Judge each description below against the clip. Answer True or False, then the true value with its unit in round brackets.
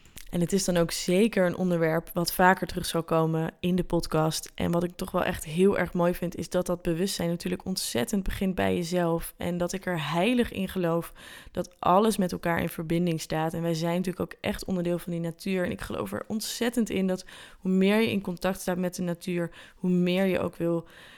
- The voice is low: False (180 Hz)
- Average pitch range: False (1.8 semitones)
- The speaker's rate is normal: False (225 wpm)